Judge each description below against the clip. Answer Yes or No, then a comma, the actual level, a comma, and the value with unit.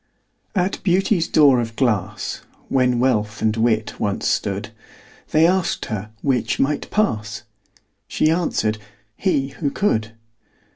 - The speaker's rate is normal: No, slow, 125 wpm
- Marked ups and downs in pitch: Yes, wide, 6.9 semitones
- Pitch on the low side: Yes, low, 125 Hz